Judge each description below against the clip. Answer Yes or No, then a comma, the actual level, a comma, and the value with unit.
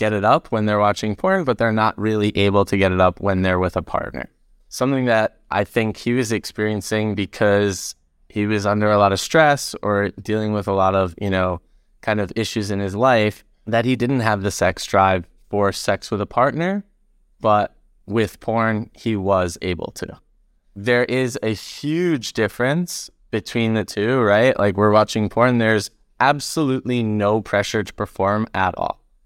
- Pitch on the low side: Yes, low, 105 Hz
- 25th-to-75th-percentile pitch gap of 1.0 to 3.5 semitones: Yes, narrow, 2.6 semitones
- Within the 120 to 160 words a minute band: No, average, 185 wpm